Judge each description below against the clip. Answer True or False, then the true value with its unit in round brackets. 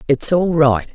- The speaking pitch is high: False (150 Hz)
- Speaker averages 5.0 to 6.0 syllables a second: False (4.1 syllables/s)